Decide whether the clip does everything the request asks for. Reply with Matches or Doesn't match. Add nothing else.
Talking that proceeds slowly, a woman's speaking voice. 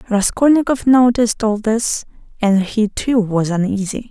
Matches